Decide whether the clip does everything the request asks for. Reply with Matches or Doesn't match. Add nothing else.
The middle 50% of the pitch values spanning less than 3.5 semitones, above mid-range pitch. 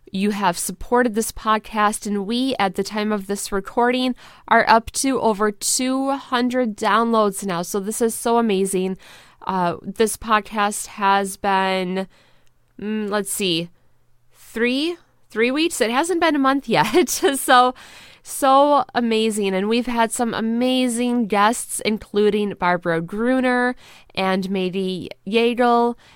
Doesn't match